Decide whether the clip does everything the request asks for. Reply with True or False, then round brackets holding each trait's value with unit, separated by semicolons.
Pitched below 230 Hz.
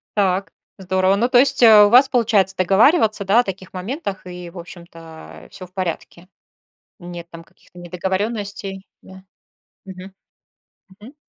True (190 Hz)